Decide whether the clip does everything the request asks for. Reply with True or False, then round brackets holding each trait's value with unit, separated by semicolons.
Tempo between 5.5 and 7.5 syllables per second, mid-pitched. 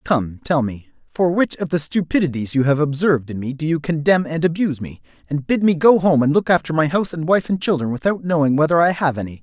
True (6.1 syllables/s; 155 Hz)